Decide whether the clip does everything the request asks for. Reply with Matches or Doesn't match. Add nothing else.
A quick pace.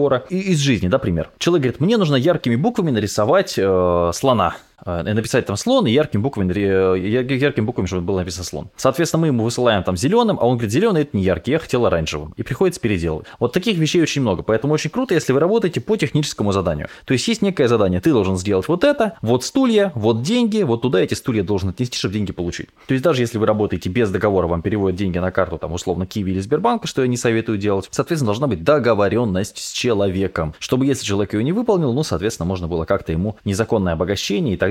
Matches